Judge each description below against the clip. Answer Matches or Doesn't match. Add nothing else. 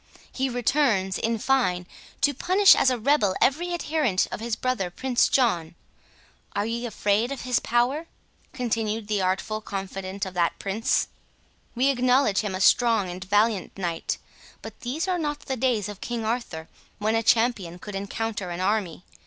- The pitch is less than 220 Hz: Doesn't match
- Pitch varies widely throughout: Doesn't match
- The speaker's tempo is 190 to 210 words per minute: Doesn't match